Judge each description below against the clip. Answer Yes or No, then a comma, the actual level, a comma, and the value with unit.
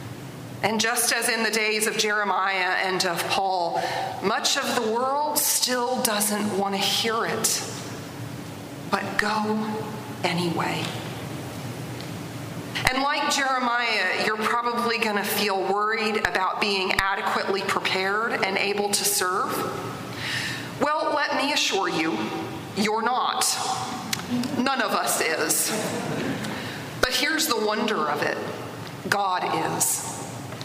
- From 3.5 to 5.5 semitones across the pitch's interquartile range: Yes, average, 4.1 semitones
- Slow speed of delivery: Yes, slow, 115 wpm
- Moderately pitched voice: No, high, 210 Hz